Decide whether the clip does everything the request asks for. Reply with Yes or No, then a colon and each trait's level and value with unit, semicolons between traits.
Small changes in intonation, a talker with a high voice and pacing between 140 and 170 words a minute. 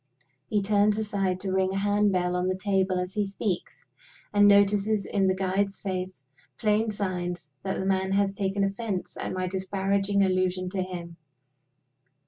Yes: narrow, 1.6 semitones; high, 195 Hz; average, 165 wpm